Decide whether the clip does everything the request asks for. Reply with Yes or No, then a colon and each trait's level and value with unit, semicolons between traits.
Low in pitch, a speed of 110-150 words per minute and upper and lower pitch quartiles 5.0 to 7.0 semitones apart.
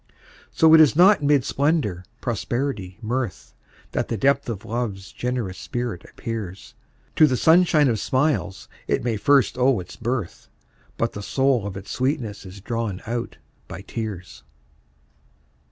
Yes: low, 120 Hz; average, 145 wpm; average, 5.3 semitones